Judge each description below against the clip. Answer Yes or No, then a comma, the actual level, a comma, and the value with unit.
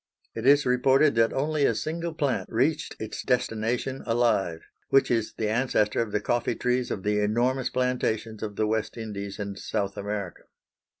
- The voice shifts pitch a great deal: No, average, 3.5 semitones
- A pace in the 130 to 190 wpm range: Yes, average, 170 wpm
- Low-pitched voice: Yes, low, 115 Hz